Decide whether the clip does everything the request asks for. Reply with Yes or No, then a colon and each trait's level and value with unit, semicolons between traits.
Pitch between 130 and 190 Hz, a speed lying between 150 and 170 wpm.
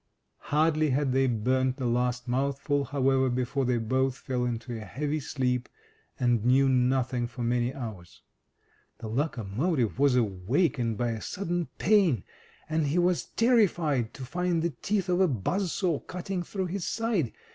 Yes: low, 135 Hz; average, 155 wpm